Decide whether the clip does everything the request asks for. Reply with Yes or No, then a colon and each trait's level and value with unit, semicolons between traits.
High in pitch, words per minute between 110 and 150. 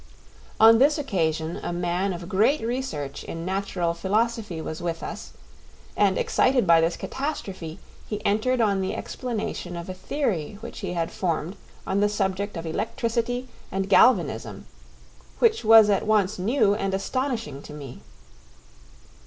Yes: high, 195 Hz; average, 145 wpm